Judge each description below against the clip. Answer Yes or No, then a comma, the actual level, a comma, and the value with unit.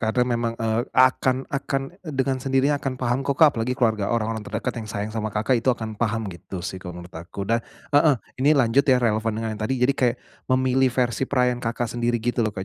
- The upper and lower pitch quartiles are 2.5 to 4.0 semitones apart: Yes, average, 3.0 semitones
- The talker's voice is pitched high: No, low, 120 Hz